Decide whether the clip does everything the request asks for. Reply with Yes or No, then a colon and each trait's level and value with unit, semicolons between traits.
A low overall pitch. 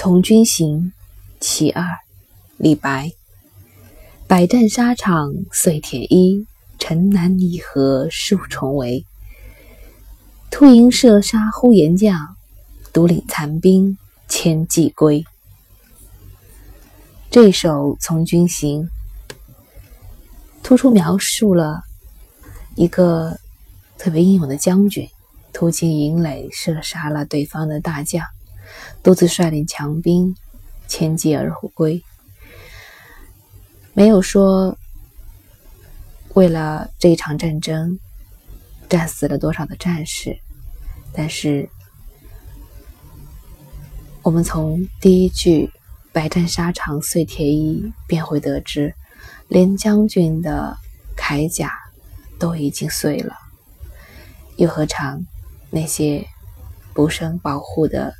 No: medium, 155 Hz